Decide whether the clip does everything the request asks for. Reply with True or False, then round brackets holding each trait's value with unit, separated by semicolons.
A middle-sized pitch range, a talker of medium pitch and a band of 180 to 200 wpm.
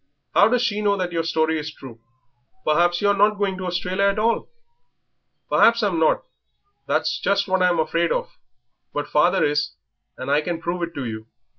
True (4.0 semitones; 175 Hz; 190 wpm)